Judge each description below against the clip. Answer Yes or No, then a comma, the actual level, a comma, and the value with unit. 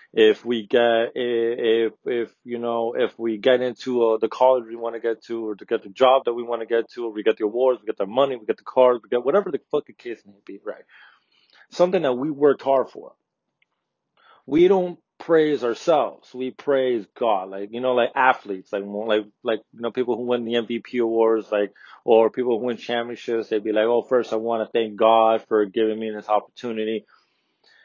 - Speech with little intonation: Yes, narrow, 2.2 semitones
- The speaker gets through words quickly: Yes, fast, 220 wpm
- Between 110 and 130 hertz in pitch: Yes, low, 115 Hz